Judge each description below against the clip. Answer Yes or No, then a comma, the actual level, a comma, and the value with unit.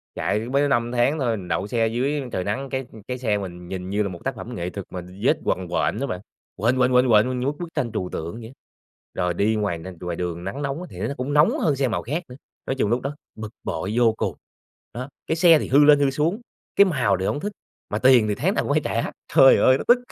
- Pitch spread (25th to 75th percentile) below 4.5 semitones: No, wide, 5.5 semitones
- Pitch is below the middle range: Yes, low, 120 Hz